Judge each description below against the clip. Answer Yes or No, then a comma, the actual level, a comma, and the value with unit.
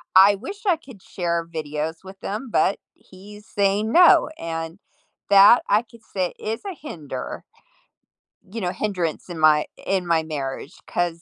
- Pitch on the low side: No, high, 190 Hz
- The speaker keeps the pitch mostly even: No, average, 4.5 semitones